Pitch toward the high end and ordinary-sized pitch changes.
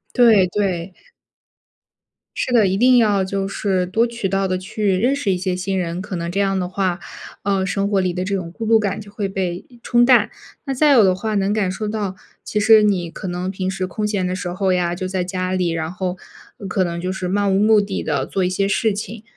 No: high, 195 Hz; narrow, 2.3 semitones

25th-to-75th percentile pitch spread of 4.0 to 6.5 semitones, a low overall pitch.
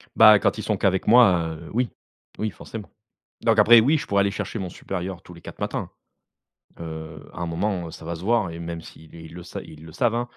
Yes: average, 4.6 semitones; very low, 90 Hz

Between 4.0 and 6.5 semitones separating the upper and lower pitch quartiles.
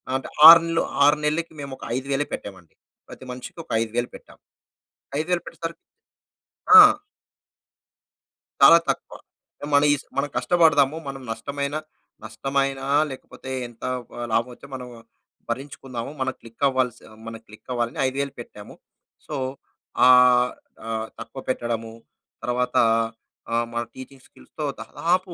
No: average, 3.2 semitones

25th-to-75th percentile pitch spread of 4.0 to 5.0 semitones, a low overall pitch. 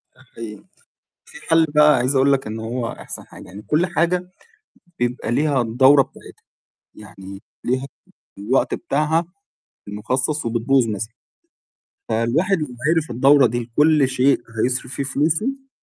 Yes: average, 4.6 semitones; low, 130 Hz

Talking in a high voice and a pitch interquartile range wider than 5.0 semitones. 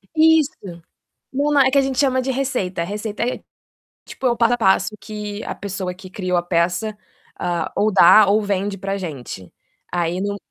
Yes: high, 205 Hz; wide, 5.4 semitones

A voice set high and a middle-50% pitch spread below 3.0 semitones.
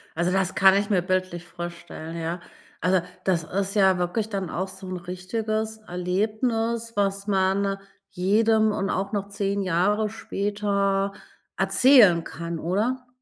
Yes: high, 195 Hz; narrow, 2.6 semitones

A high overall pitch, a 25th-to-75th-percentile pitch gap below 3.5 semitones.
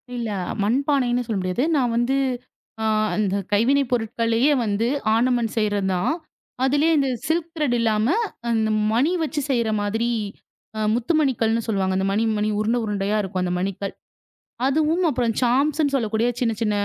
No: high, 230 Hz; average, 4.2 semitones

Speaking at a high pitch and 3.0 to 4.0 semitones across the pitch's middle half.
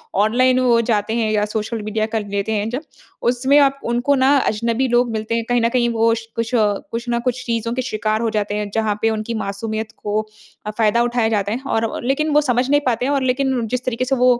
No: high, 230 Hz; narrow, 2.6 semitones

